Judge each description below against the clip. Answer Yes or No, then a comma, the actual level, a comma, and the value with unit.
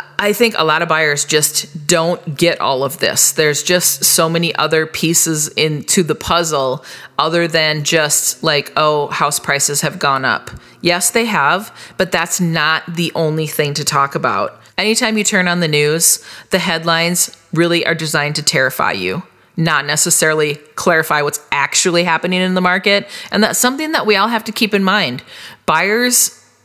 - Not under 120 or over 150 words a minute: No, average, 175 wpm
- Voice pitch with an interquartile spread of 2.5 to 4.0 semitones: Yes, average, 3.2 semitones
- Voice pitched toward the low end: No, medium, 165 Hz